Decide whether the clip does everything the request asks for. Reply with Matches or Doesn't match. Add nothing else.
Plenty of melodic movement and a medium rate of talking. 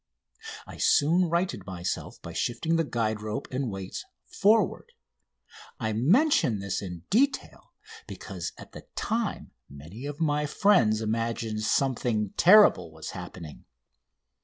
Doesn't match